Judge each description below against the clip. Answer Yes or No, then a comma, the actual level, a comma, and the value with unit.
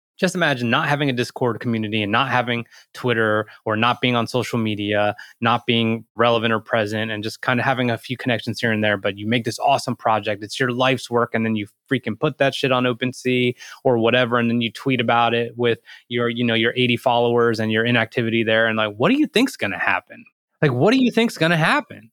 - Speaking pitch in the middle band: No, low, 120 Hz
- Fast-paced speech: Yes, fast, 235 wpm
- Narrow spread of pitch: Yes, narrow, 2.2 semitones